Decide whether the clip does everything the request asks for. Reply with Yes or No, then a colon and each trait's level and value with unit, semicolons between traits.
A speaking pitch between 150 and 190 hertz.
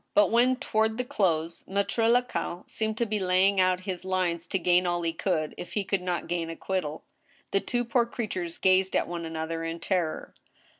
Yes: medium, 185 Hz